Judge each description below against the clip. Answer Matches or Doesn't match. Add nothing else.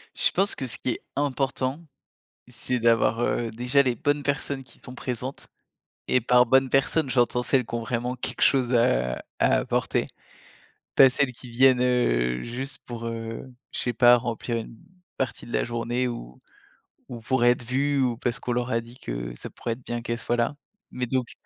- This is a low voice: Matches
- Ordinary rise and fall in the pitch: Doesn't match